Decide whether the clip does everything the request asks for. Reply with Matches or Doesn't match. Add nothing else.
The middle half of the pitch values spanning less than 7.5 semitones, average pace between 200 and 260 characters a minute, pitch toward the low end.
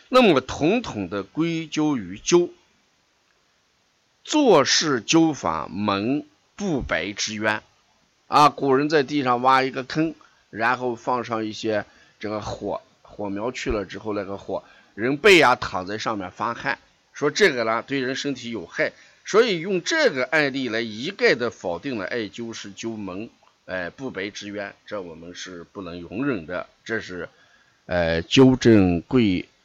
Matches